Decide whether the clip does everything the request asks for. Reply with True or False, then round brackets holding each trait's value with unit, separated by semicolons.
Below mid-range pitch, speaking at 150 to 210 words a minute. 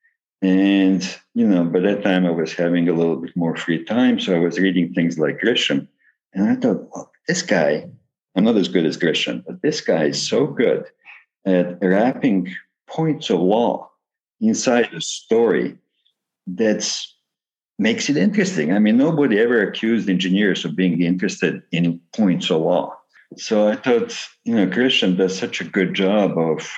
True (95 Hz; 175 wpm)